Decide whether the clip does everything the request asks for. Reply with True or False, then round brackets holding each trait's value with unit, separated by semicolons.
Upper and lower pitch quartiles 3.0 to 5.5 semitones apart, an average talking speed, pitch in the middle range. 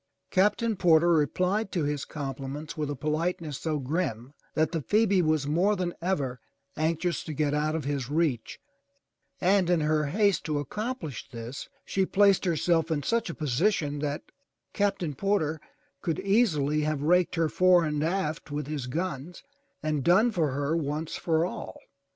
True (3.8 semitones; 165 wpm; 160 Hz)